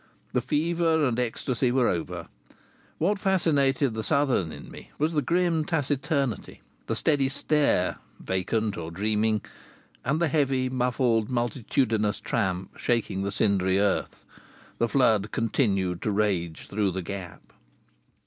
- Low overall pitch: Yes, low, 120 Hz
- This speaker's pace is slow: Yes, slow, 130 wpm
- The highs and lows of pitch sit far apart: Yes, wide, 6.0 semitones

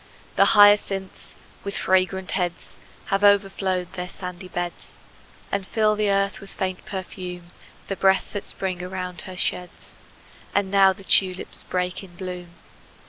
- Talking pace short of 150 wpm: Yes, average, 140 wpm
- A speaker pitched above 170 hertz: Yes, high, 190 Hz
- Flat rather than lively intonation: Yes, narrow, 1.5 semitones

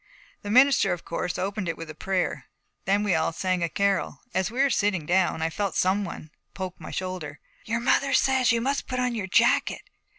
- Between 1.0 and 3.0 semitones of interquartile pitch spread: No, average, 4.7 semitones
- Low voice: No, high, 195 Hz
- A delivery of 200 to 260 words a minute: Yes, fast, 205 wpm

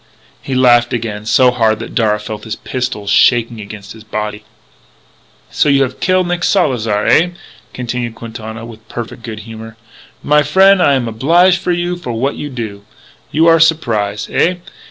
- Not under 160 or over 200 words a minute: Yes, average, 170 wpm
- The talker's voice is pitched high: No, low, 120 Hz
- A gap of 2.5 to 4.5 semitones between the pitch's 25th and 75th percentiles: No, average, 5.1 semitones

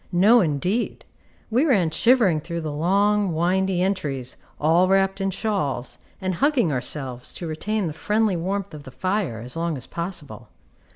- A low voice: No, medium, 180 Hz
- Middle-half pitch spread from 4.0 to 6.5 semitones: Yes, average, 4.6 semitones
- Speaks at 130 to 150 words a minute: No, average, 160 wpm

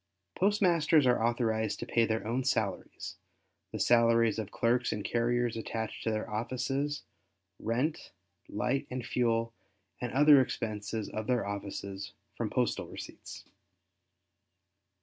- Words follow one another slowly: Yes, slow, 125 wpm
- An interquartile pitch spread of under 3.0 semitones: Yes, narrow, 2.5 semitones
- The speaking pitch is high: No, low, 115 Hz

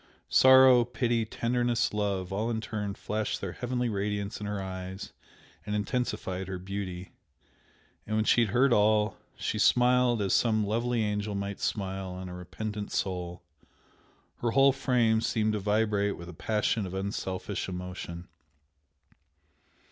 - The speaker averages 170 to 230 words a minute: No, average, 145 wpm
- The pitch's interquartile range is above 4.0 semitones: No, average, 3.4 semitones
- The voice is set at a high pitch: No, low, 105 Hz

